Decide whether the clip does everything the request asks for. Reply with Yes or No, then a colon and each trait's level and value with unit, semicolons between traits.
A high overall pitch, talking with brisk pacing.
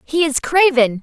No: very high, 290 Hz; average, 175 wpm